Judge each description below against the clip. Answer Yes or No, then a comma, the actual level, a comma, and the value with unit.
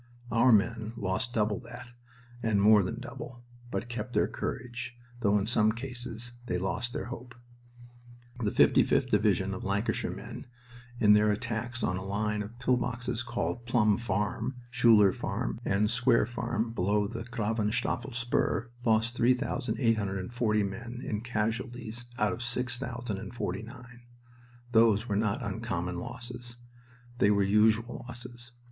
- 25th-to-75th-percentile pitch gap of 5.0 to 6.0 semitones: No, narrow, 2.5 semitones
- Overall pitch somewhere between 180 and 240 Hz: No, low, 115 Hz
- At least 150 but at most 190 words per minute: No, slow, 135 wpm